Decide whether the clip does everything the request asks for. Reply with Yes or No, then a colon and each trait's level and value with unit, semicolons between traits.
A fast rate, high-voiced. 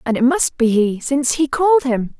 Yes: fast, 245 wpm; very high, 265 Hz